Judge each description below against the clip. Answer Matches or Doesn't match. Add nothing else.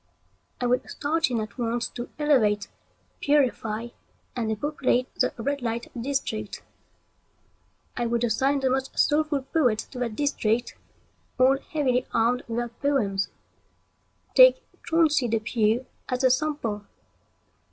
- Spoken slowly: Matches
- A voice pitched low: Doesn't match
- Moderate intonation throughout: Matches